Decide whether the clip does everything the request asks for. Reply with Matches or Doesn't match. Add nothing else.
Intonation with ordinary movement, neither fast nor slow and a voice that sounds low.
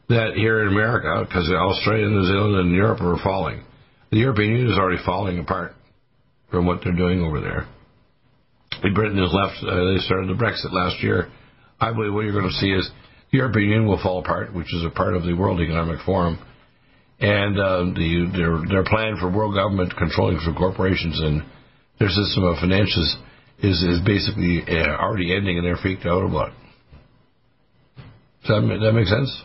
Matches